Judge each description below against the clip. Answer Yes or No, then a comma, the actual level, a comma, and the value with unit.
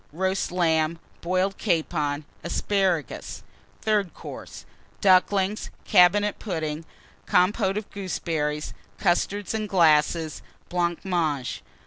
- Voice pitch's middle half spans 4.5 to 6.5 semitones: No, average, 3.5 semitones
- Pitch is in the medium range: Yes, medium, 180 Hz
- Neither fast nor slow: No, slow, 85 wpm